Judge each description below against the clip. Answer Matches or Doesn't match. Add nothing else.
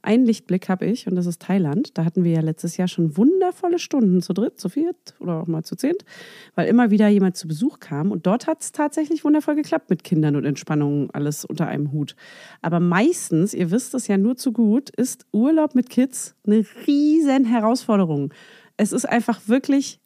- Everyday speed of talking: Doesn't match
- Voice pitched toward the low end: Doesn't match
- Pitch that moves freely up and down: Matches